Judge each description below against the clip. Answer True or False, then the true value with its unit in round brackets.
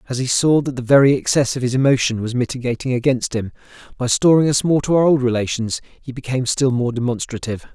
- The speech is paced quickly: True (210 wpm)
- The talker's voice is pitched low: True (125 Hz)